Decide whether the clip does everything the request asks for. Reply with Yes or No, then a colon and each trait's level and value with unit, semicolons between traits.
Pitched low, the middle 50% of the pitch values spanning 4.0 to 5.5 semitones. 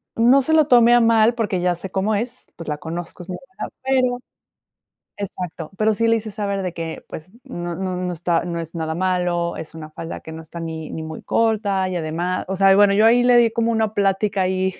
No: high, 190 Hz; average, 4.6 semitones